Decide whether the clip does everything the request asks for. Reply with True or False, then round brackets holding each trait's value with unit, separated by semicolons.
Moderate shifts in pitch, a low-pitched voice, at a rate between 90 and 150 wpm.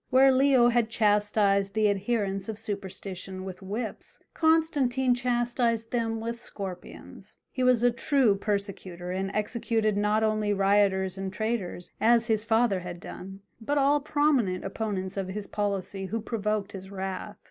False (3.6 semitones; 210 Hz; 145 wpm)